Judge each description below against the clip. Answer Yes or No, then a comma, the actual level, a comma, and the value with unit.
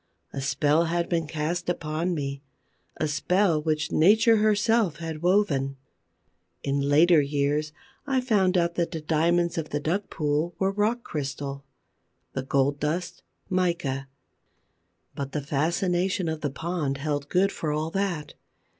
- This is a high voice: No, medium, 160 Hz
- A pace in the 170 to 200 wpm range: No, average, 140 wpm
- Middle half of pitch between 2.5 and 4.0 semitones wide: Yes, average, 3.7 semitones